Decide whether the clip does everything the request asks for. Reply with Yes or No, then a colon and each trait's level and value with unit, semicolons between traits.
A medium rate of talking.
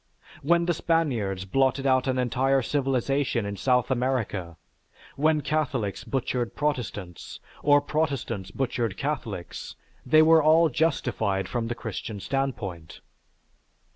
No: slow, 115 wpm